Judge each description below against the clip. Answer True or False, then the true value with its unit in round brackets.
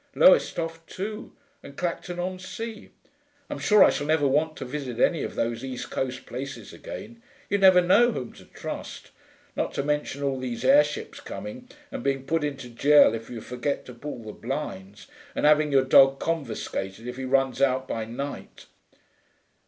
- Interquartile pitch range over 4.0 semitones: True (5.3 semitones)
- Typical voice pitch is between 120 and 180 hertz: True (140 Hz)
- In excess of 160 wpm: True (175 wpm)